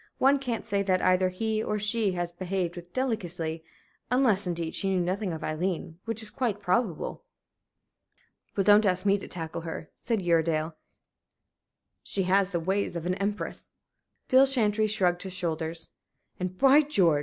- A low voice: No, high, 190 Hz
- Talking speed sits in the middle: Yes, average, 165 wpm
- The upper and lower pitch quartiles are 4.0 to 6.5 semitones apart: No, average, 3.6 semitones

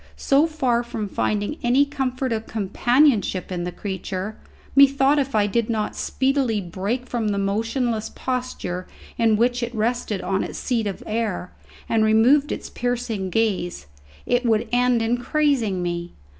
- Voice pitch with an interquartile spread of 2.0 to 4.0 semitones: Yes, average, 3.6 semitones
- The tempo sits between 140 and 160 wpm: Yes, average, 155 wpm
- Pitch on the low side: No, high, 230 Hz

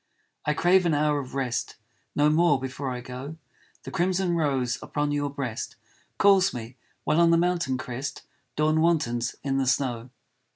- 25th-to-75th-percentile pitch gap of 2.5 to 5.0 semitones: Yes, average, 4.5 semitones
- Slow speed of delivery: No, average, 165 wpm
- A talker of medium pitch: Yes, medium, 145 Hz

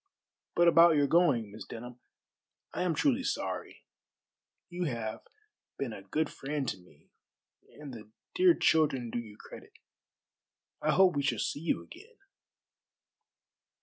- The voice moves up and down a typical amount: No, wide, 6.6 semitones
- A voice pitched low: No, medium, 145 Hz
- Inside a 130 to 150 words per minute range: Yes, average, 140 wpm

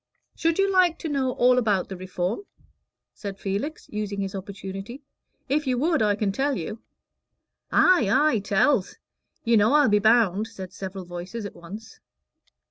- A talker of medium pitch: No, high, 215 Hz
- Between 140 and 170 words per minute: Yes, average, 160 wpm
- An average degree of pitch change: No, wide, 5.8 semitones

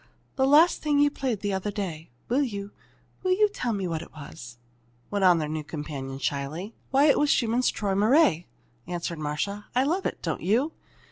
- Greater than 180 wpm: Yes, average, 190 wpm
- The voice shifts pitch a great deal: Yes, wide, 9.0 semitones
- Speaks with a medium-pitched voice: No, high, 200 Hz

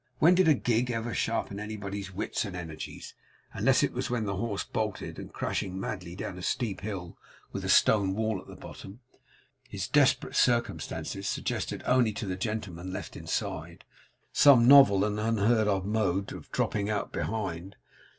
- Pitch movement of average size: Yes, average, 3.2 semitones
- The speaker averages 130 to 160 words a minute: No, average, 170 wpm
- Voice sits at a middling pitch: No, low, 105 Hz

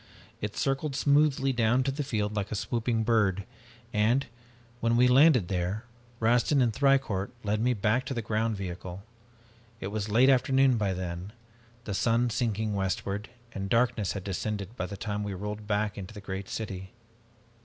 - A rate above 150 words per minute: Yes, average, 170 wpm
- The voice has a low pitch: Yes, low, 110 Hz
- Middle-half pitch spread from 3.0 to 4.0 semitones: Yes, average, 3.7 semitones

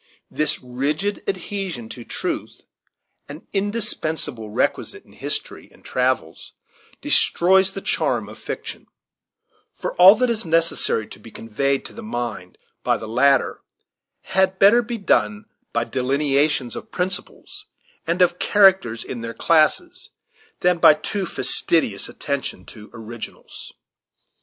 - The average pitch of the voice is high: No, medium, 155 Hz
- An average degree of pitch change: No, wide, 8.1 semitones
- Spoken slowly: Yes, slow, 130 wpm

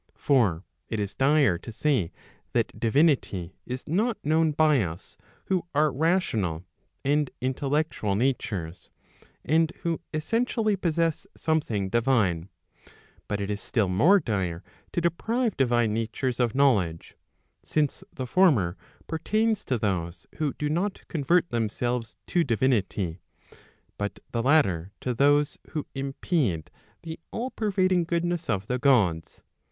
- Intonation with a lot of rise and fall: Yes, wide, 7.8 semitones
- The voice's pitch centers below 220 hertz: Yes, low, 135 Hz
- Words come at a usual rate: No, slow, 130 wpm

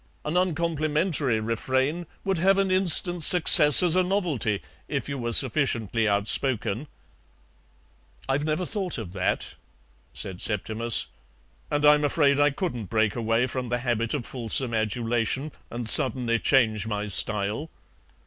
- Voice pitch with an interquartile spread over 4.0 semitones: Yes, wide, 5.5 semitones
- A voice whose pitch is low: Yes, low, 130 Hz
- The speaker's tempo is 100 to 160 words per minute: Yes, slow, 135 wpm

